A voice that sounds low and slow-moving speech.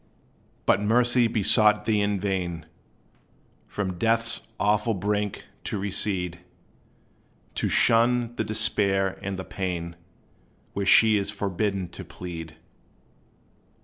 Yes: low, 100 Hz; slow, 110 wpm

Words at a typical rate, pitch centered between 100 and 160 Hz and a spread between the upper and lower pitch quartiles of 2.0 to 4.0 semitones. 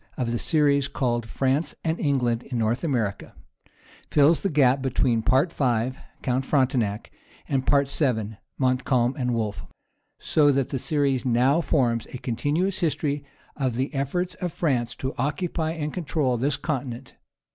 Yes: average, 150 wpm; low, 135 Hz; average, 3.4 semitones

